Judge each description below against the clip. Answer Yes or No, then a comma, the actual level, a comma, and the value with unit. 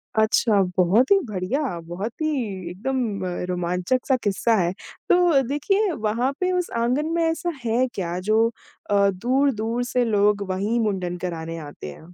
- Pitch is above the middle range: Yes, high, 220 Hz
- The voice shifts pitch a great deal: Yes, wide, 6.1 semitones